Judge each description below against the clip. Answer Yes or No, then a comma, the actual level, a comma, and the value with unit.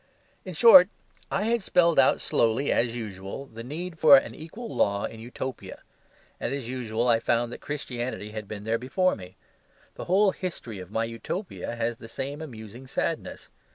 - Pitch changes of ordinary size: No, wide, 6.0 semitones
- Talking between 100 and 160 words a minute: No, average, 175 wpm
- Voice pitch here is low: Yes, low, 125 Hz